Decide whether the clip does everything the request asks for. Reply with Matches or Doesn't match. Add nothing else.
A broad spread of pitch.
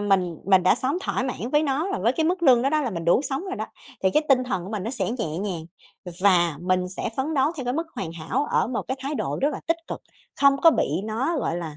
Matches